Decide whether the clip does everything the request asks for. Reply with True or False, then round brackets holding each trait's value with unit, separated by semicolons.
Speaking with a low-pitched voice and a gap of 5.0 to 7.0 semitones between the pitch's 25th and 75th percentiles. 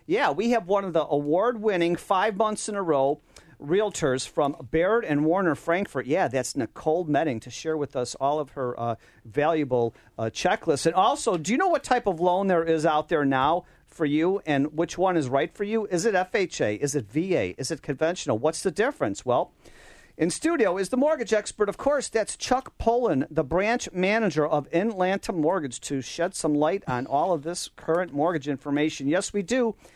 False (165 Hz; 5.5 semitones)